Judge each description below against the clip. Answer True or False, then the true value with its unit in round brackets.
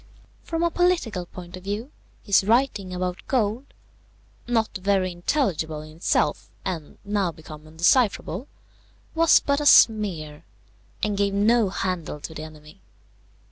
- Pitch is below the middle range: False (195 Hz)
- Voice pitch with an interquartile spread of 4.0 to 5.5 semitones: True (5.1 semitones)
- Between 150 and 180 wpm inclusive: False (135 wpm)